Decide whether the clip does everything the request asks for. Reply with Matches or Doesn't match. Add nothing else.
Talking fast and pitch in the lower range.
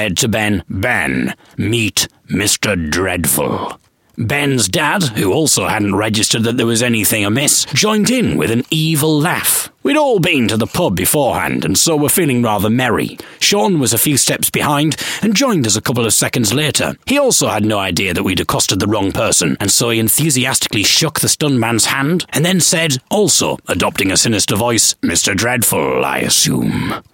Doesn't match